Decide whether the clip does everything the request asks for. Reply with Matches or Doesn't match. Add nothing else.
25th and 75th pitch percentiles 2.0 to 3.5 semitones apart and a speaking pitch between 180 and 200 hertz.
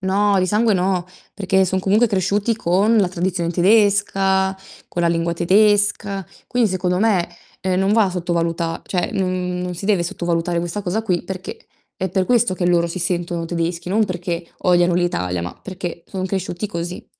Matches